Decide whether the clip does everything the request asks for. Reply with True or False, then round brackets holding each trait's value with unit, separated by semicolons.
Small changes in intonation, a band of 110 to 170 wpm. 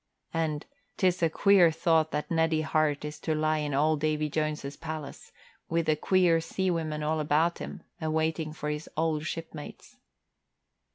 True (1.3 semitones; 160 wpm)